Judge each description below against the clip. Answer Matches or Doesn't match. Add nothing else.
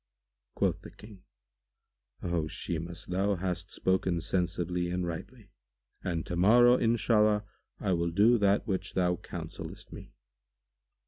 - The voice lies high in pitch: Doesn't match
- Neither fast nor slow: Doesn't match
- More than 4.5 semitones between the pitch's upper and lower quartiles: Doesn't match